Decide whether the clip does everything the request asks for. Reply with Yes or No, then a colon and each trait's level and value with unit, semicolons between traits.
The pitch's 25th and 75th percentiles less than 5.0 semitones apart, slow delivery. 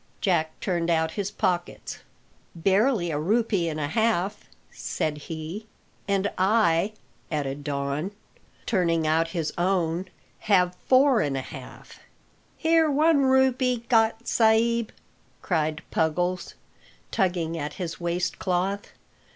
No: wide, 5.4 semitones; slow, 120 wpm